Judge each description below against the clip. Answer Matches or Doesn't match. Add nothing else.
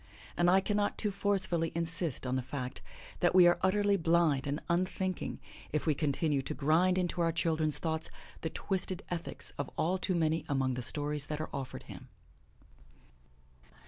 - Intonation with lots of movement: Doesn't match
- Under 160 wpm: Doesn't match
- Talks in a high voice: Doesn't match